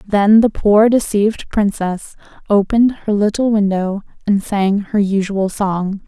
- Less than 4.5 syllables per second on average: Yes, 4.2 syllables/s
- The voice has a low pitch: No, high, 205 Hz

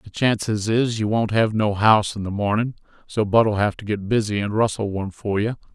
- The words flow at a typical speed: No, fast, 230 wpm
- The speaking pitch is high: No, low, 105 Hz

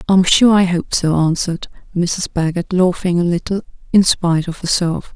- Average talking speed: Yes, average, 175 wpm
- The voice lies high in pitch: No, medium, 175 Hz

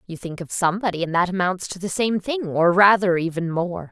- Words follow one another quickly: Yes, fast, 230 wpm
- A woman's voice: Yes, female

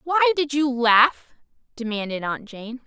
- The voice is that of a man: No, female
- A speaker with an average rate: Yes, average, 145 wpm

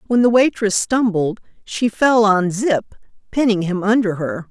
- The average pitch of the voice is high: Yes, high, 210 Hz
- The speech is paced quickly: No, average, 160 wpm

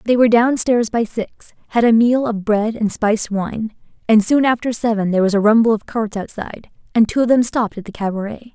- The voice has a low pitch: No, high, 220 Hz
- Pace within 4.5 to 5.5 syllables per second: No, 5.7 syllables/s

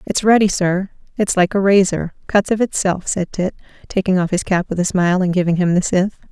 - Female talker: Yes, female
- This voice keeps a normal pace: No, fast, 230 wpm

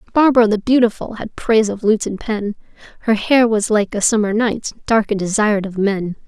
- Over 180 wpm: Yes, average, 200 wpm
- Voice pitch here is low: No, high, 215 Hz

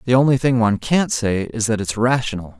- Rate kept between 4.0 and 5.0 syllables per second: No, 5.8 syllables/s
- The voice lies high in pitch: No, low, 115 Hz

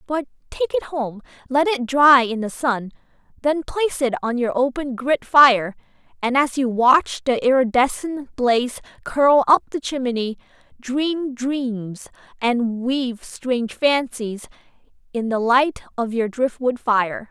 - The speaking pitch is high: Yes, very high, 255 Hz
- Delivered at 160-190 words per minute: No, average, 145 wpm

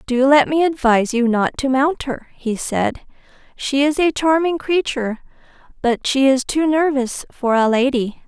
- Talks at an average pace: Yes, average, 175 wpm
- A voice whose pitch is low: No, very high, 265 Hz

